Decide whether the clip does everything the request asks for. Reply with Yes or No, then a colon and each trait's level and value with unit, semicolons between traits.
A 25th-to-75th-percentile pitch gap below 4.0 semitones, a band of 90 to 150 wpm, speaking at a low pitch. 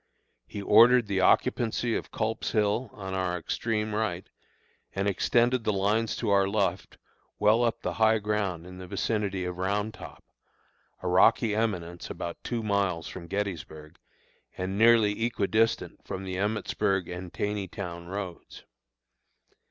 Yes: average, 3.0 semitones; average, 145 wpm; low, 100 Hz